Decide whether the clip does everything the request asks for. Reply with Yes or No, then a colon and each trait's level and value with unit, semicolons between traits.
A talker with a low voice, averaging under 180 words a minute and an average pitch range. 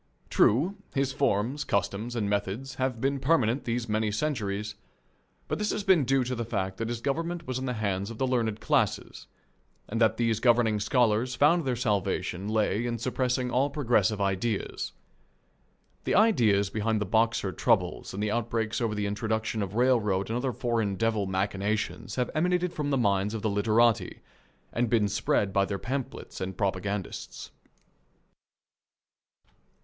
Yes: low, 115 Hz; average, 160 wpm; average, 3.8 semitones